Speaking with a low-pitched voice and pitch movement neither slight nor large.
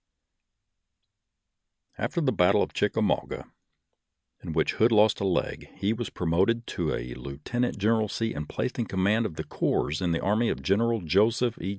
Yes: low, 105 Hz; average, 4.7 semitones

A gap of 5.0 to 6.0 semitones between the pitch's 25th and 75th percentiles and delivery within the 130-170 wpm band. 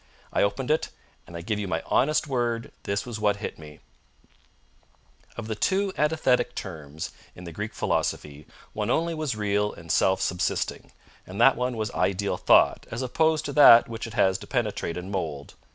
No: average, 5.3 semitones; average, 185 wpm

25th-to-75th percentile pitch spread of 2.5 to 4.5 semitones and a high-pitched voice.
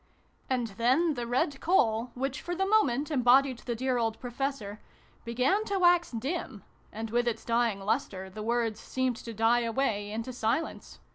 Yes: average, 3.3 semitones; high, 240 Hz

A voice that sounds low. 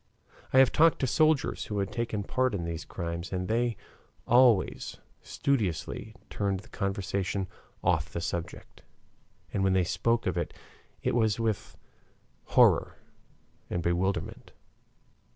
Yes: low, 100 Hz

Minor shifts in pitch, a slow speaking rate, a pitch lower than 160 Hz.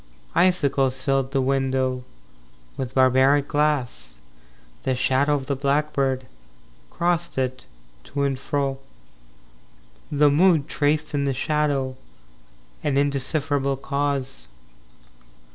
Yes: narrow, 1.8 semitones; slow, 105 wpm; medium, 140 Hz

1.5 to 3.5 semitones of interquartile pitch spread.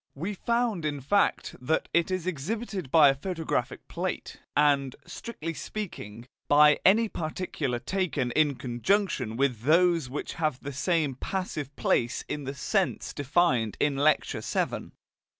No: average, 5.2 semitones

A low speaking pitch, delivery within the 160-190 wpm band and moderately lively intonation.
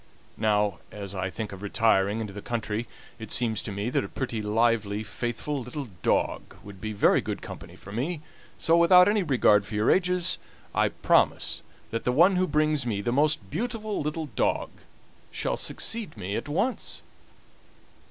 No: low, 120 Hz; average, 170 wpm; wide, 6.8 semitones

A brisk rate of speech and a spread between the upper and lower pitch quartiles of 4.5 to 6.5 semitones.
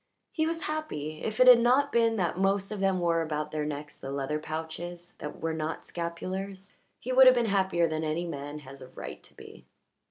Yes: fast, 215 wpm; wide, 5.6 semitones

